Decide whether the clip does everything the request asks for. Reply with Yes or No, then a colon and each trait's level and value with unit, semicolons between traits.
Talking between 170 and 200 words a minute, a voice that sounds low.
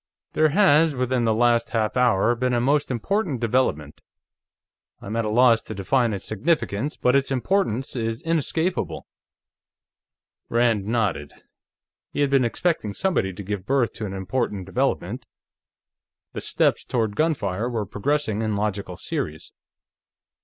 No: average, 145 wpm; low, 120 Hz